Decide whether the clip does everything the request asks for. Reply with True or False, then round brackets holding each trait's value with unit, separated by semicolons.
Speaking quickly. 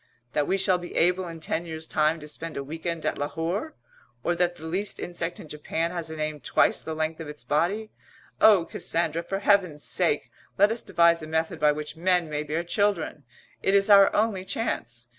True (210 wpm)